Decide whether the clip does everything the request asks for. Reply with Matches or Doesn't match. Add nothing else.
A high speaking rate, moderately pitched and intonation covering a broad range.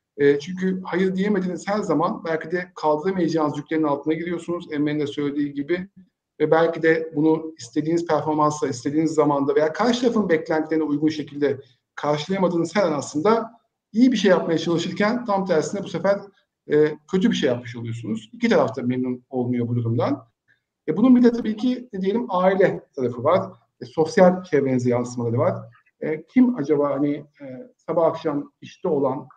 Doesn't match